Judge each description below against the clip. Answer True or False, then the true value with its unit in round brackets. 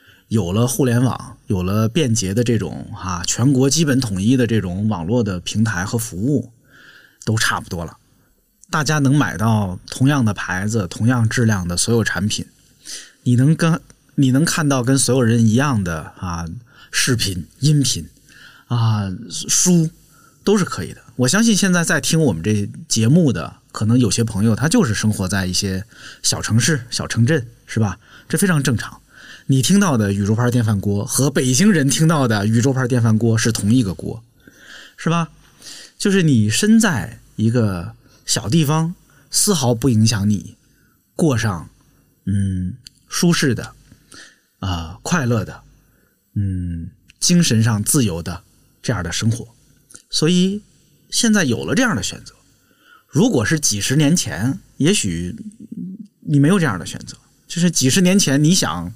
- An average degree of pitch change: False (6.2 semitones)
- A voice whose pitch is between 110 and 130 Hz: True (120 Hz)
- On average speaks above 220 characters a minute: True (230 characters per minute)